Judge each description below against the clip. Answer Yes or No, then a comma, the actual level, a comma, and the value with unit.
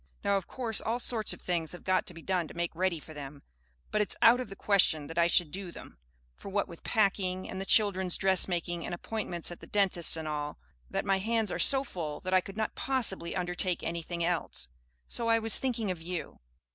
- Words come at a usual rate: No, fast, 225 wpm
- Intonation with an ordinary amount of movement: Yes, average, 3.5 semitones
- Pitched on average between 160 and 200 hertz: Yes, medium, 185 Hz